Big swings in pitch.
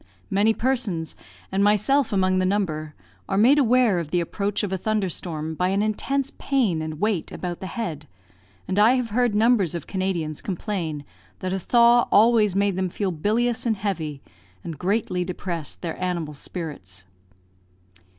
No: average, 4.3 semitones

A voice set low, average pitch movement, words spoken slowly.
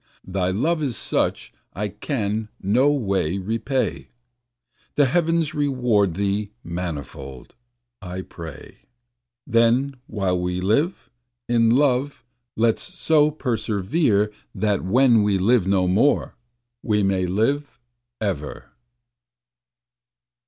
No: low, 110 Hz; wide, 6.0 semitones; slow, 105 wpm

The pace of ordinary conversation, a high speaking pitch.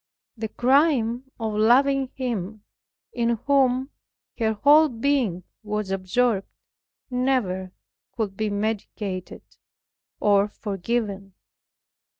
No: slow, 90 wpm; high, 225 Hz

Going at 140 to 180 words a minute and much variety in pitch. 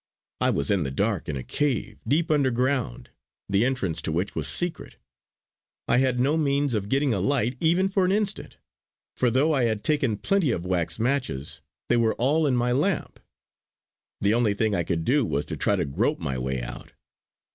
No: average, 195 wpm; wide, 6.6 semitones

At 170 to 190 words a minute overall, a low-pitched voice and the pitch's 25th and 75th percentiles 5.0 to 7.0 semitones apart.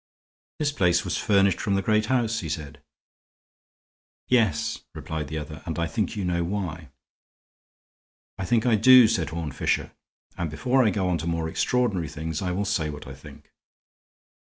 Yes: average, 175 wpm; very low, 90 Hz; wide, 5.4 semitones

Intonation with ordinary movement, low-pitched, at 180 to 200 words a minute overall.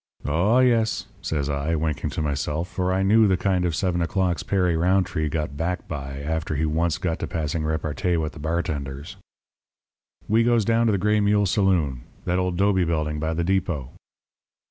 Yes: average, 3.8 semitones; very low, 85 Hz; average, 185 wpm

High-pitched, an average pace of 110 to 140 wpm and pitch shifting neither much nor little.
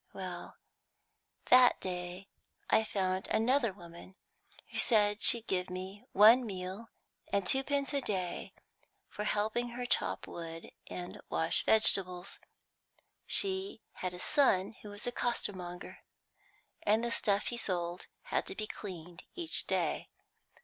Yes: high, 205 Hz; slow, 135 wpm; average, 4.5 semitones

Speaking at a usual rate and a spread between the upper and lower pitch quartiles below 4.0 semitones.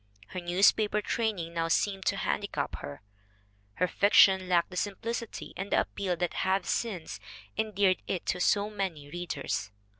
Yes: average, 150 wpm; average, 2.7 semitones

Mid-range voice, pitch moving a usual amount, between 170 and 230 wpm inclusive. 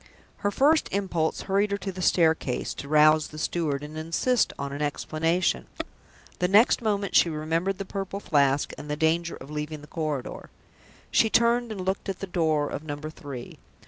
Yes: medium, 165 Hz; average, 4.6 semitones; average, 185 wpm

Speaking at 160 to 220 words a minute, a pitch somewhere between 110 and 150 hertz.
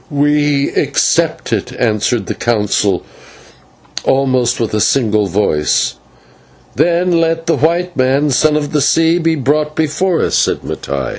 No: slow, 135 wpm; medium, 140 Hz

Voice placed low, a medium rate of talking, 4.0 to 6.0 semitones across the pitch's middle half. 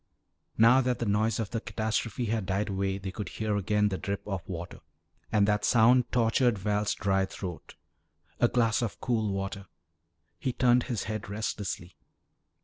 No: low, 105 Hz; average, 165 wpm; average, 2.7 semitones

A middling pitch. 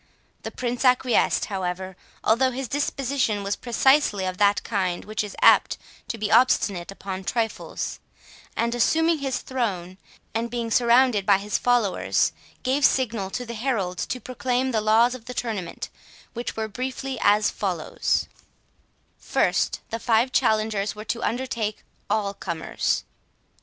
No: high, 225 Hz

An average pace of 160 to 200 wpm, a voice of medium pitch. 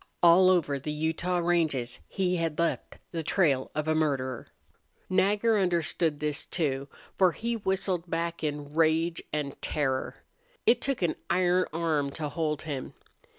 No: average, 150 wpm; medium, 165 Hz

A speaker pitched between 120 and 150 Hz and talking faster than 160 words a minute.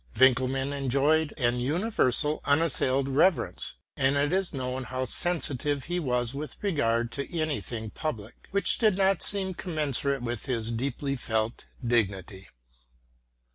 No: low, 135 Hz; slow, 135 wpm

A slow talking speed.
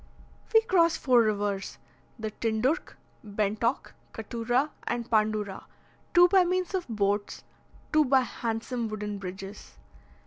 Yes: slow, 115 wpm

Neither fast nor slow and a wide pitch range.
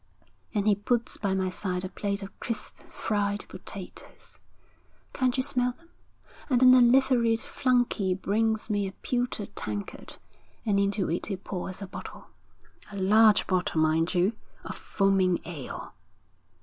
No: average, 150 wpm; average, 3.9 semitones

